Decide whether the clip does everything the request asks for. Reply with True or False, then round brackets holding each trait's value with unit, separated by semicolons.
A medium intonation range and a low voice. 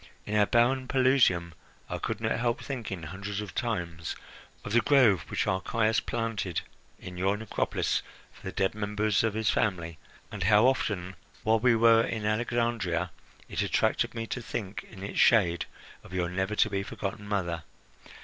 True (3.4 semitones; 105 Hz)